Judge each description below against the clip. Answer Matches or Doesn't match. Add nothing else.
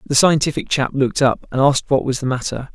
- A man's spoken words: Matches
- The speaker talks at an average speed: Doesn't match